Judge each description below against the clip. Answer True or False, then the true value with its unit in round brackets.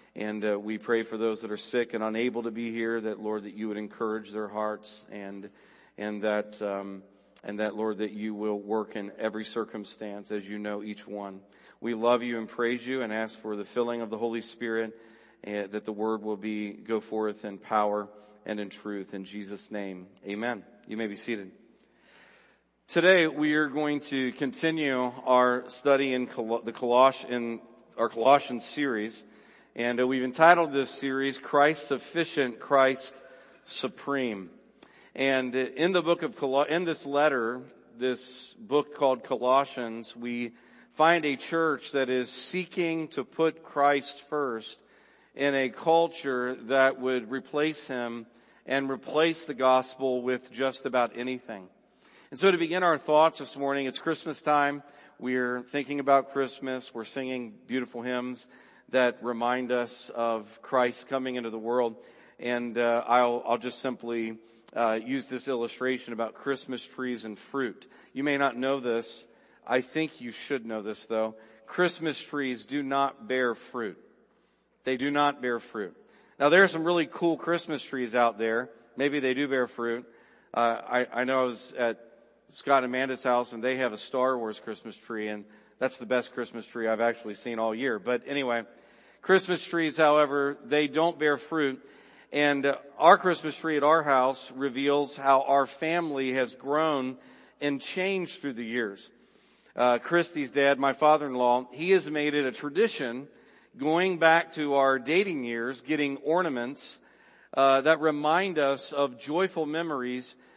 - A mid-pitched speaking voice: False (125 Hz)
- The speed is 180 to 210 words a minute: False (165 wpm)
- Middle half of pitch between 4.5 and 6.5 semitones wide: False (3.8 semitones)